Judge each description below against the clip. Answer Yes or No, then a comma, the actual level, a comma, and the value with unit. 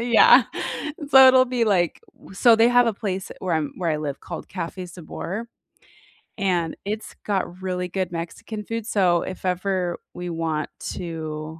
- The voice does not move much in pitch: No, average, 4.2 semitones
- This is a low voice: No, medium, 185 Hz